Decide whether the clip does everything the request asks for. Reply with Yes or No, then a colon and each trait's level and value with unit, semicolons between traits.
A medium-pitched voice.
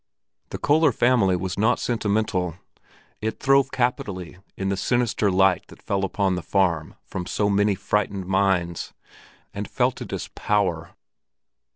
No: low, 100 Hz